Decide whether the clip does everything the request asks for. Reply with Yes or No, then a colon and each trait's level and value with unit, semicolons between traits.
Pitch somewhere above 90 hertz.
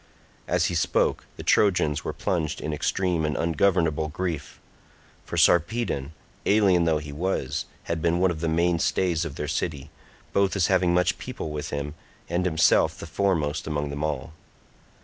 No: very low, 80 Hz